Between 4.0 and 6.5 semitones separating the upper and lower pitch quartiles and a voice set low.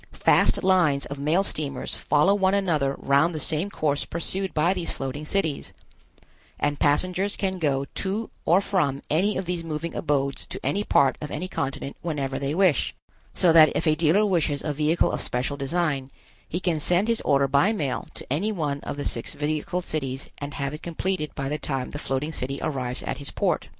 No: average, 4.3 semitones; medium, 155 Hz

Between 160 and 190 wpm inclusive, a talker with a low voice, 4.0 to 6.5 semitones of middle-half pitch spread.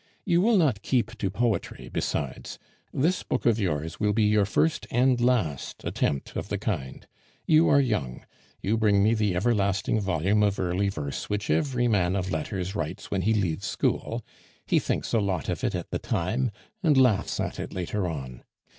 Yes: average, 185 wpm; low, 105 Hz; average, 5.1 semitones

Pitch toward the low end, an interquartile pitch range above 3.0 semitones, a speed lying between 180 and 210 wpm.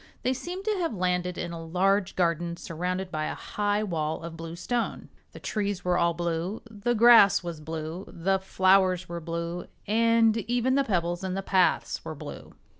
No: medium, 185 Hz; average, 3.8 semitones; average, 185 wpm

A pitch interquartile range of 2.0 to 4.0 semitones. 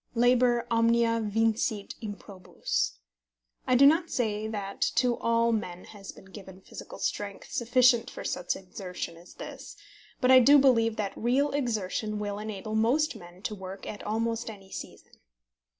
Yes: average, 3.2 semitones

